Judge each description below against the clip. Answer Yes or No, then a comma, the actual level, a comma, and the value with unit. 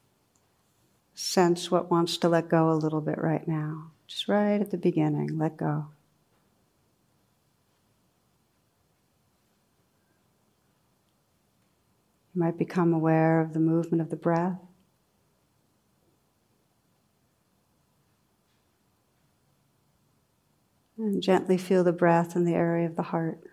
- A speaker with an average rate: No, slow, 100 wpm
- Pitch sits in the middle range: Yes, medium, 170 Hz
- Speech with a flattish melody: Yes, narrow, 1.9 semitones